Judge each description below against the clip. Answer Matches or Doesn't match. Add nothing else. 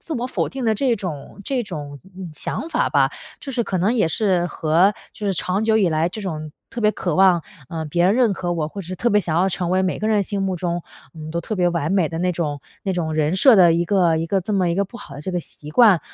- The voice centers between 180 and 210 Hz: Matches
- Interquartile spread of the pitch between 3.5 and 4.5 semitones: Matches